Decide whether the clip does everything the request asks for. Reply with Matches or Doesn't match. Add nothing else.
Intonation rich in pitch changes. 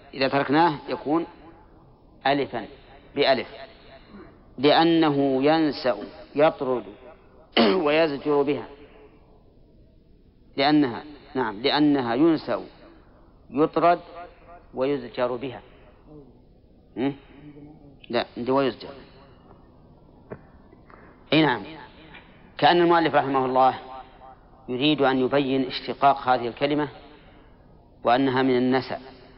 Doesn't match